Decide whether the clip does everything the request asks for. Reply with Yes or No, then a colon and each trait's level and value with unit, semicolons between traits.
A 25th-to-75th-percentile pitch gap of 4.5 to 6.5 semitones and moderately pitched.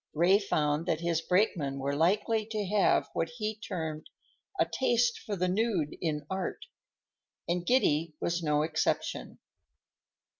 Yes: average, 5.1 semitones; medium, 175 Hz